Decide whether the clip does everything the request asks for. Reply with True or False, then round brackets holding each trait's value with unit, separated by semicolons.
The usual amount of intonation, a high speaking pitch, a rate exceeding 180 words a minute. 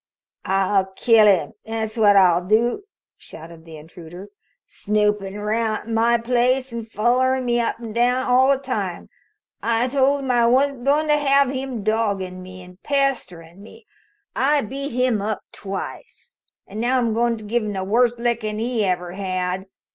False (4.4 semitones; 225 Hz; 165 wpm)